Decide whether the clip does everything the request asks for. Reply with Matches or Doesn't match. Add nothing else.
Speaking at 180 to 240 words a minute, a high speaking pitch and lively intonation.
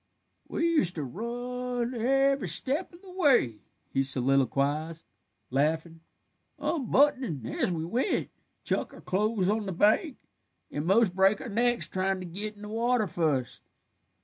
Doesn't match